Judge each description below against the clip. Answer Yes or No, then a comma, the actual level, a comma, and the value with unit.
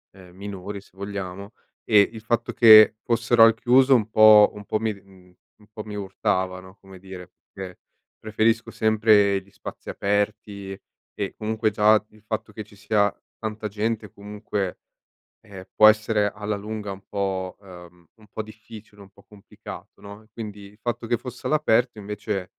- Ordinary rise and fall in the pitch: No, narrow, 1.8 semitones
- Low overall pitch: Yes, low, 105 Hz